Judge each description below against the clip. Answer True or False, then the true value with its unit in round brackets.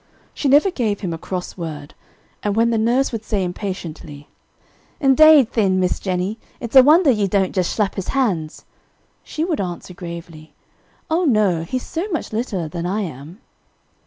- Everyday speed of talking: True (170 wpm)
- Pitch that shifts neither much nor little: False (6.4 semitones)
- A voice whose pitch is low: False (200 Hz)